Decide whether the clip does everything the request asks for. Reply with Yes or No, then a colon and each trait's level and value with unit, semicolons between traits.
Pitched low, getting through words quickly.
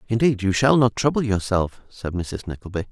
No: low, 105 Hz; average, 185 wpm